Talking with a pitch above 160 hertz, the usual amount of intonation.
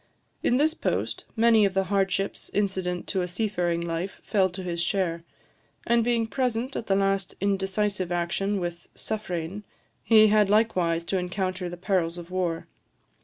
Yes: high, 190 Hz; average, 3.0 semitones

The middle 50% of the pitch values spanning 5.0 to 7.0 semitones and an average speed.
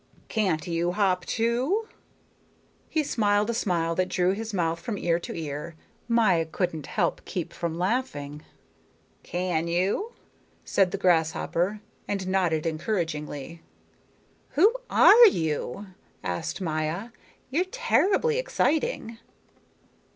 No: wide, 5.5 semitones; slow, 110 wpm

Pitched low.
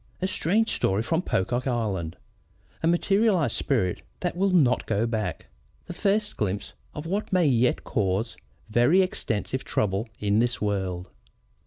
Yes: low, 120 Hz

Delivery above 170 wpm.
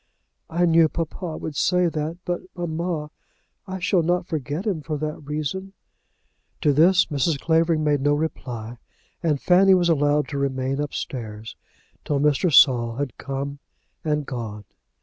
No: average, 150 wpm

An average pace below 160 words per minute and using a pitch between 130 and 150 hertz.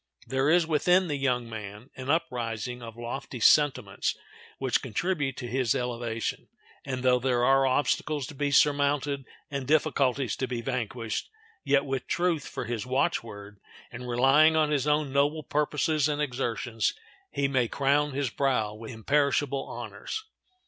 Yes: average, 150 wpm; low, 135 Hz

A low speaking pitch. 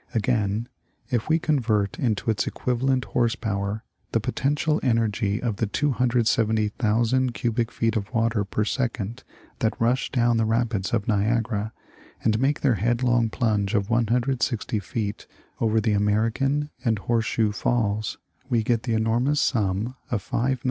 Yes: low, 115 Hz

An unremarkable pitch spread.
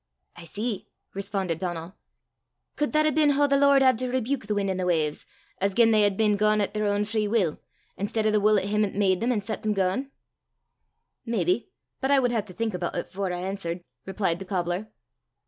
Yes: average, 3.5 semitones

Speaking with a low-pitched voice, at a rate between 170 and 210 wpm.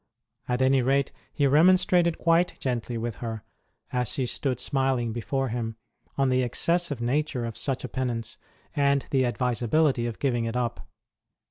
No: low, 130 Hz; average, 155 wpm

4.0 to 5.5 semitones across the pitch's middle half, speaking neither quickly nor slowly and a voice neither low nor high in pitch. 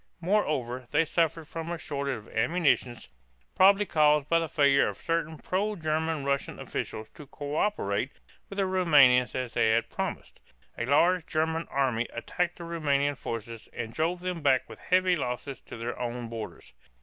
Yes: average, 5.1 semitones; average, 165 wpm; medium, 150 Hz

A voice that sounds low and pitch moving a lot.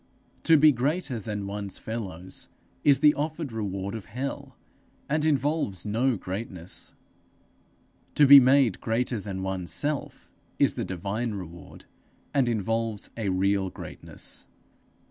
Yes: low, 115 Hz; wide, 6.1 semitones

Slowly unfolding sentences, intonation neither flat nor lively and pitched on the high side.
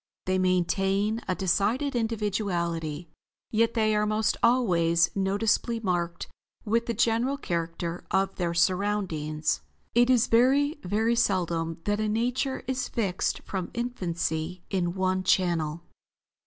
Yes: slow, 125 wpm; average, 4.8 semitones; high, 195 Hz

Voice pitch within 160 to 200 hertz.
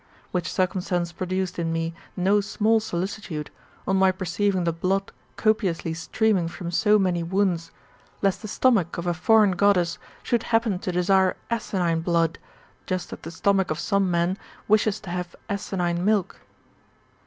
Yes: medium, 185 Hz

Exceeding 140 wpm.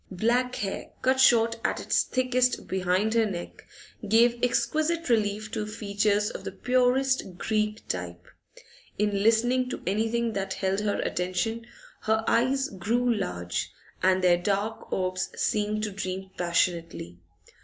No: slow, 135 wpm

